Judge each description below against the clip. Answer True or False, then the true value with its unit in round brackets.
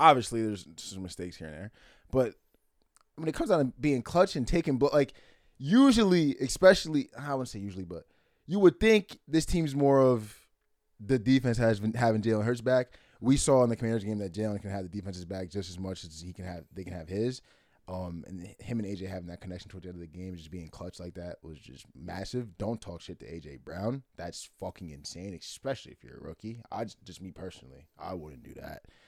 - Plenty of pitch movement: True (6.4 semitones)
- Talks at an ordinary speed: False (230 wpm)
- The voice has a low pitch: True (105 Hz)